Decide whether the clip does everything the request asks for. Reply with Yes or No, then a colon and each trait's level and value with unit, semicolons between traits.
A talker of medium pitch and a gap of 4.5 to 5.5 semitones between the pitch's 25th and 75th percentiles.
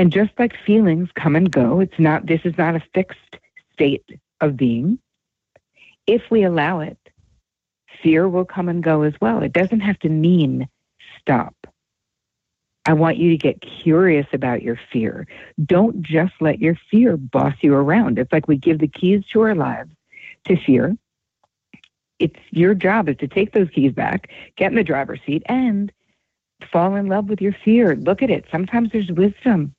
Yes: medium, 175 Hz; average, 4.8 semitones